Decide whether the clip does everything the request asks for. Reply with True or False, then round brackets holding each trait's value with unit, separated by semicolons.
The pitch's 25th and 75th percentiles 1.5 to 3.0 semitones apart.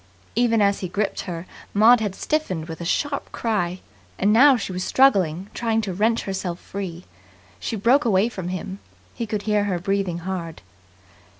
False (3.8 semitones)